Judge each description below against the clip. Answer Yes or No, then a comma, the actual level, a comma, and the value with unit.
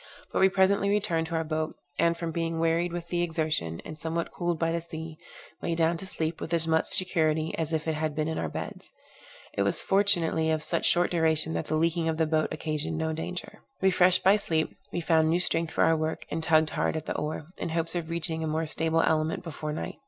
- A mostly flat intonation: Yes, narrow, 1.3 semitones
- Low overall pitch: No, medium, 160 Hz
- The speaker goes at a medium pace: No, fast, 235 wpm